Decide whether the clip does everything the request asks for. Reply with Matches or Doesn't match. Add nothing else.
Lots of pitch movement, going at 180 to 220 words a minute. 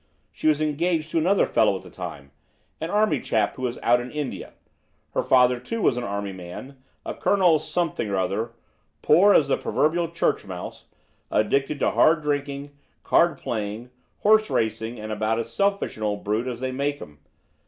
Matches